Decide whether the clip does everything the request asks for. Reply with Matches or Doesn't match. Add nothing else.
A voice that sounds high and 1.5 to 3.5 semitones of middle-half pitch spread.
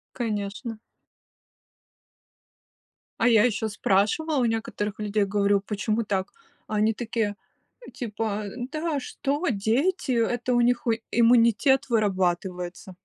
Matches